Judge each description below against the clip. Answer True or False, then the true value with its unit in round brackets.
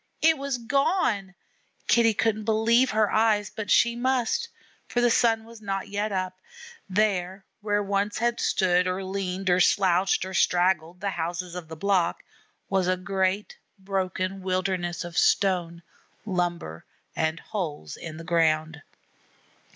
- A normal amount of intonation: True (3.3 semitones)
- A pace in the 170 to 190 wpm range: False (145 wpm)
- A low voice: False (190 Hz)